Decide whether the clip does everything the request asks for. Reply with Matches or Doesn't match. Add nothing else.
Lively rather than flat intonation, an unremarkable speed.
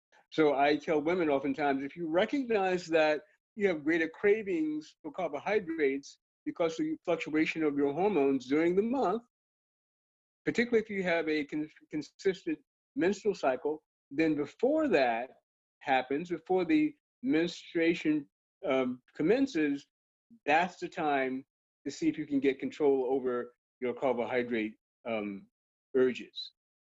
Doesn't match